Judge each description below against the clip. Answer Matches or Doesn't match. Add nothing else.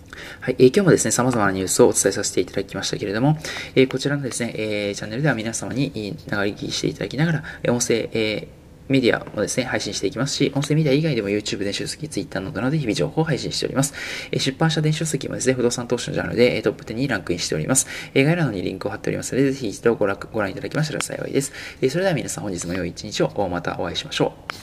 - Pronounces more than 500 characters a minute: Matches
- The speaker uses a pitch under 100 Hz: Doesn't match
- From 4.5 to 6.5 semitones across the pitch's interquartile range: Matches